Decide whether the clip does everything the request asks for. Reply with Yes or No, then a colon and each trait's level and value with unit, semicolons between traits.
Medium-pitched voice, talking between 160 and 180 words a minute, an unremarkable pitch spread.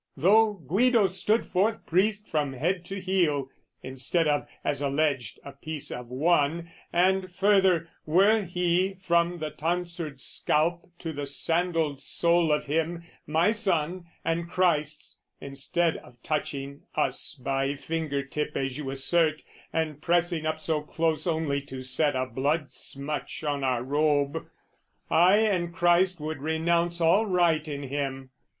No: medium, 160 Hz; average, 145 wpm; average, 3.6 semitones